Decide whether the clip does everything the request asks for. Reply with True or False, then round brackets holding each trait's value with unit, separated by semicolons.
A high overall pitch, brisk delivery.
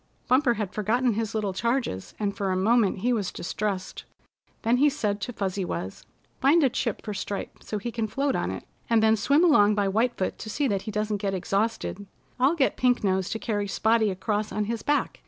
True (215 Hz; 215 wpm)